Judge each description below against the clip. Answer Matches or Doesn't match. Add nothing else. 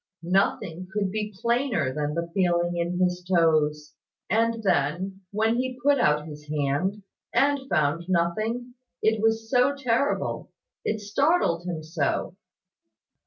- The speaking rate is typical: Doesn't match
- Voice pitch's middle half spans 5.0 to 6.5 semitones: Matches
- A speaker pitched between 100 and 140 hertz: Doesn't match